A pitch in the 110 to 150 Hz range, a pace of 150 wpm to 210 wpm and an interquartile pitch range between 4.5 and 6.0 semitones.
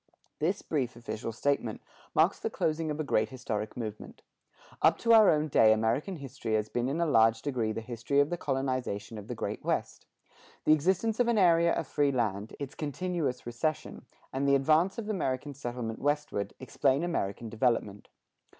Yes: low, 135 Hz; average, 175 wpm; wide, 5.5 semitones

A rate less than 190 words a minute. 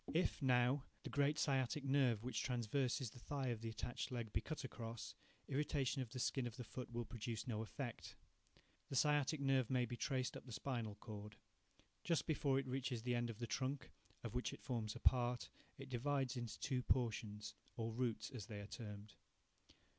No: average, 195 wpm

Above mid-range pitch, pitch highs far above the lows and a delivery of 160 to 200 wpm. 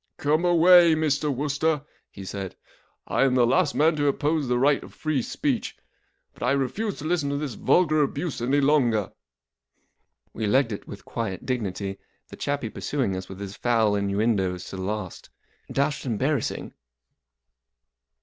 No: low, 135 Hz; wide, 6.0 semitones; average, 165 wpm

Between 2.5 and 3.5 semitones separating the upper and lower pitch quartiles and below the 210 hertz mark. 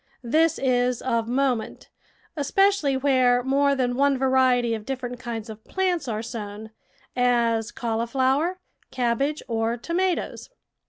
No: average, 3.1 semitones; very high, 250 Hz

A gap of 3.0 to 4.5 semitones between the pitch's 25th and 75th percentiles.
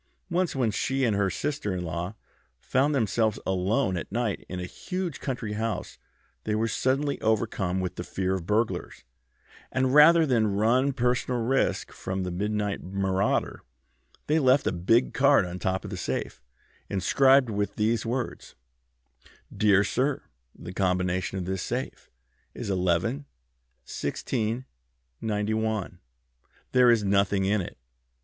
No: average, 5.2 semitones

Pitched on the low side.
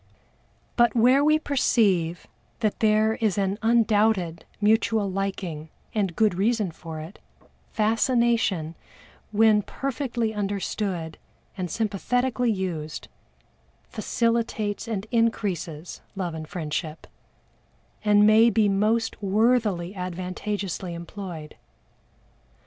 No: high, 205 Hz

